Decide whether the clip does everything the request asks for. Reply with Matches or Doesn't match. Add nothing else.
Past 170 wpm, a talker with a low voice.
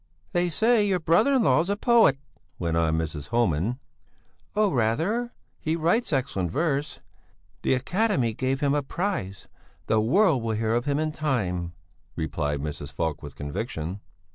Doesn't match